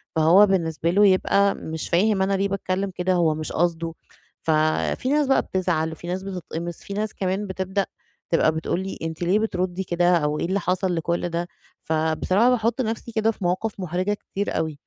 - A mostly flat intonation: No, average, 3.1 semitones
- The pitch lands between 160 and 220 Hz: Yes, medium, 185 Hz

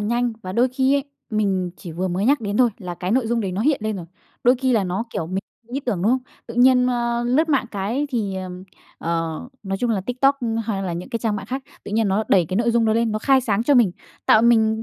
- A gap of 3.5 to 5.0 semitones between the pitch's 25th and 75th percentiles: Yes, average, 4.3 semitones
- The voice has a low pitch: No, high, 225 Hz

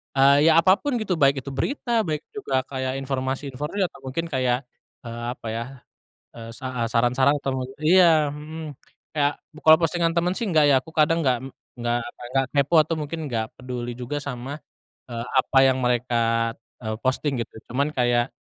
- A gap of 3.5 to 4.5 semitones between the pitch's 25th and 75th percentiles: Yes, average, 4.2 semitones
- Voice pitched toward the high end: No, low, 135 Hz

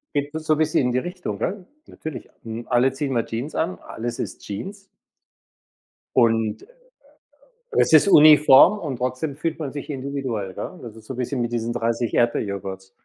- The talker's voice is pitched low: Yes, low, 130 Hz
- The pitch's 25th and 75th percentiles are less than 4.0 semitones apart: No, average, 4.8 semitones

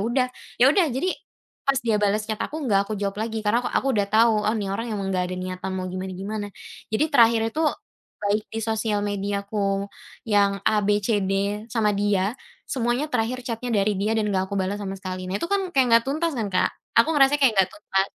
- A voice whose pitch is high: Yes, high, 210 Hz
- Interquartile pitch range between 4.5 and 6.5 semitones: No, average, 3.0 semitones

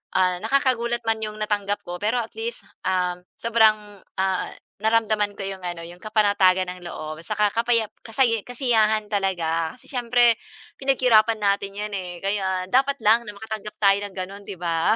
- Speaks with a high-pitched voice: Yes, high, 210 Hz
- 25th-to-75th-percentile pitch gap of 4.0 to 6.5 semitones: No, average, 3.3 semitones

